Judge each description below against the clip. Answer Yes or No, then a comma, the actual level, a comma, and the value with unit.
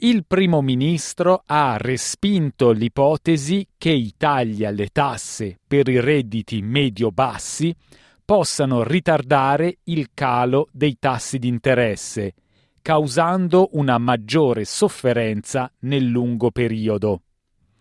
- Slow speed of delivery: Yes, slow, 100 wpm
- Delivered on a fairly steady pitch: No, average, 5.1 semitones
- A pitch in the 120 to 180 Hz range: Yes, low, 135 Hz